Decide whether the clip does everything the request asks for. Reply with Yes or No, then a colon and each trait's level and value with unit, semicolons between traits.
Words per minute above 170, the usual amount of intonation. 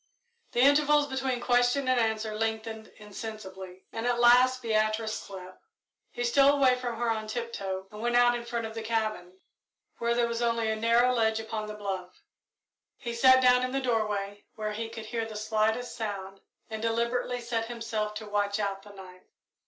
No: average, 185 wpm; narrow, 2.2 semitones